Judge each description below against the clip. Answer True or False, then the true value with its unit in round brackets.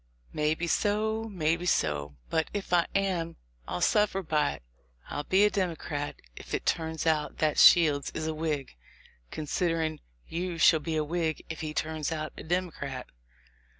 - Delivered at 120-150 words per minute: False (170 wpm)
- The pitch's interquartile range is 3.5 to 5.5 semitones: False (2.6 semitones)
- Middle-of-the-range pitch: True (160 Hz)